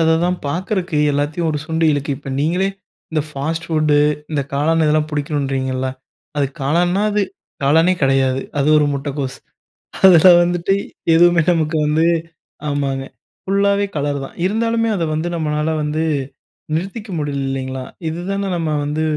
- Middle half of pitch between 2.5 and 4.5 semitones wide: Yes, average, 3.5 semitones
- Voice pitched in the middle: Yes, medium, 155 Hz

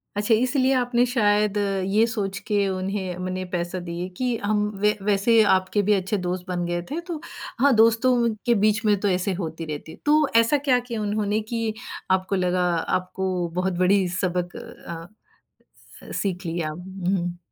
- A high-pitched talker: Yes, high, 195 Hz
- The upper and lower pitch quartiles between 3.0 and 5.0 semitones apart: Yes, average, 3.6 semitones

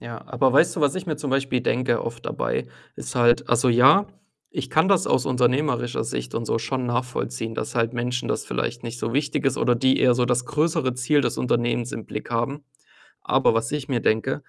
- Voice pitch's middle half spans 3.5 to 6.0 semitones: No, narrow, 2.4 semitones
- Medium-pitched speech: No, low, 125 Hz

